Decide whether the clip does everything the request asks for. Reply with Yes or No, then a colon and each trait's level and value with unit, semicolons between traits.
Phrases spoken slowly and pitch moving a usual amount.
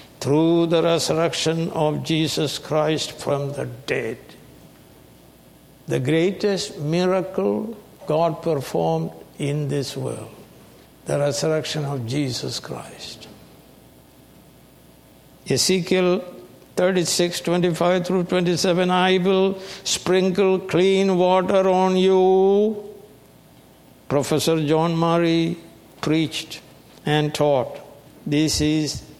Yes: slow, 85 wpm; average, 3.7 semitones